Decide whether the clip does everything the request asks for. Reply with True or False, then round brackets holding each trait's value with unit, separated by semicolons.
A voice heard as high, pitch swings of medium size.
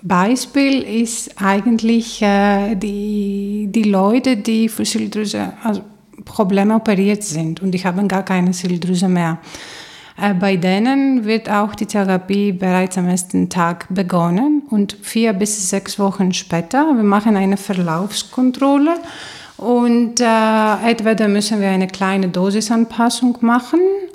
True (205 Hz; 3.1 semitones)